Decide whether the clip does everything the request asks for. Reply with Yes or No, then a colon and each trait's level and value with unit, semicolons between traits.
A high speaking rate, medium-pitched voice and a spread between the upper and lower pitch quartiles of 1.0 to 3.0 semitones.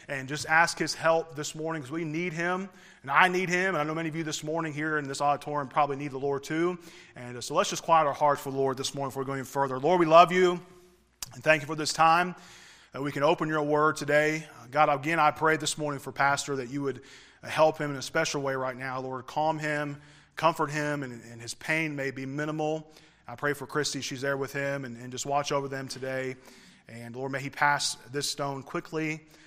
Yes: fast, 245 wpm; medium, 150 Hz; narrow, 2.6 semitones